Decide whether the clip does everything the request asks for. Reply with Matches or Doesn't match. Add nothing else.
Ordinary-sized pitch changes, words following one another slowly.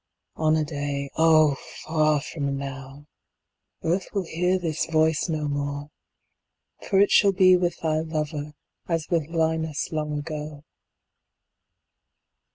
Doesn't match